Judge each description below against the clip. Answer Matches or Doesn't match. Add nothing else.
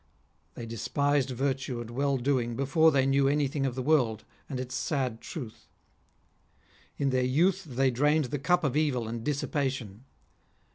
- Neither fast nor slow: Matches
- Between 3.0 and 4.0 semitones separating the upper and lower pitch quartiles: Doesn't match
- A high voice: Doesn't match